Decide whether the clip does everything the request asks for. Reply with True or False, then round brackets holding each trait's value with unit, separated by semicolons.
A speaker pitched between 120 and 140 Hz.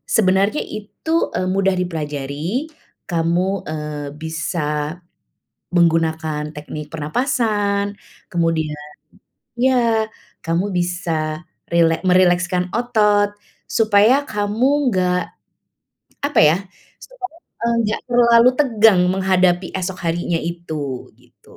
False (180 Hz)